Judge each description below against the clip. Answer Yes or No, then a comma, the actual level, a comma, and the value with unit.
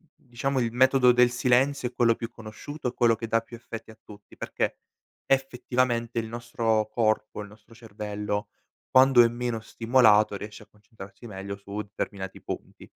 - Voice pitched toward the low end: Yes, low, 115 Hz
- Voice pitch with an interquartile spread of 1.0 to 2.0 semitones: No, narrow, 2.4 semitones